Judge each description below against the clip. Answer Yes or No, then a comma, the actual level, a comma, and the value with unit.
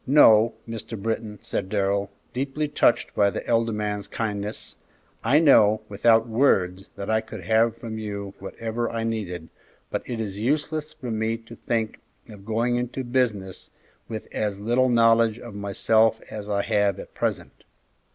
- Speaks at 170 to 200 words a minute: No, average, 160 wpm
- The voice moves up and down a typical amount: No, narrow, 2.3 semitones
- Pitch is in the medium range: No, low, 110 Hz